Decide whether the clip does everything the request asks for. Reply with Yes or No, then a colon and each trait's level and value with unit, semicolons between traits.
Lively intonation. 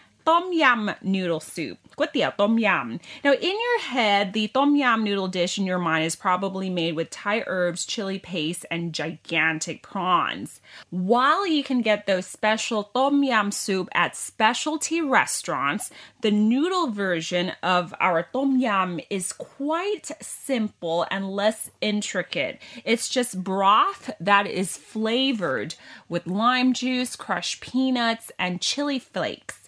Yes: wide, 6.3 semitones